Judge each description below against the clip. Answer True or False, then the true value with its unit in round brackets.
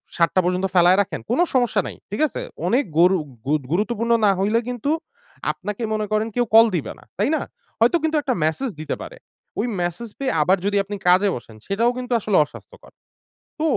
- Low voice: False (210 Hz)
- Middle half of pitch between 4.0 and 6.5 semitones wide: True (4.8 semitones)